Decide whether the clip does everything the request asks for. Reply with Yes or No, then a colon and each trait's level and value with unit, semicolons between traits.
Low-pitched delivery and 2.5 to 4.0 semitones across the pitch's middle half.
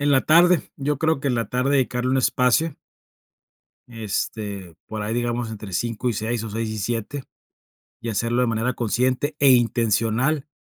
Yes: low, 120 Hz; average, 3.0 semitones